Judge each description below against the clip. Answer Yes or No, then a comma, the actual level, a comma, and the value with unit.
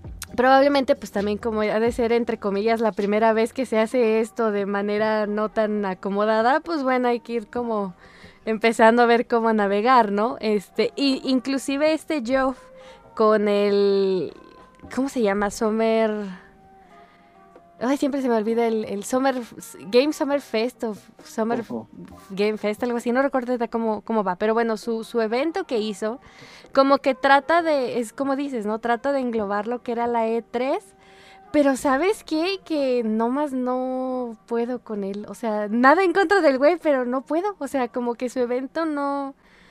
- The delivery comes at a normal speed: Yes, average, 175 wpm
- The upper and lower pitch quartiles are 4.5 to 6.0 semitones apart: No, average, 3.8 semitones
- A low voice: No, high, 235 Hz